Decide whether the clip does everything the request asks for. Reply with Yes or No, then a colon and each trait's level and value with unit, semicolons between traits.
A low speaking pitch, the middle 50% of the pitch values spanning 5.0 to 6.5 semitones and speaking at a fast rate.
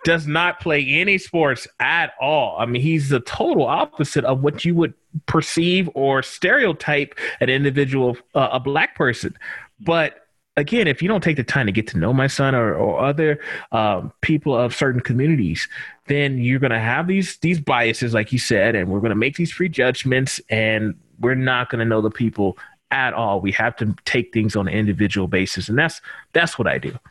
Yes: low, 130 Hz; average, 5.3 semitones; fast, 215 wpm